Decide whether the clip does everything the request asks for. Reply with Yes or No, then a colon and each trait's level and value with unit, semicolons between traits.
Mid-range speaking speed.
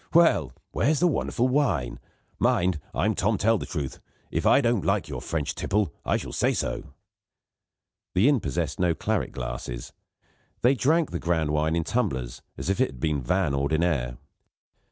Yes: average, 170 wpm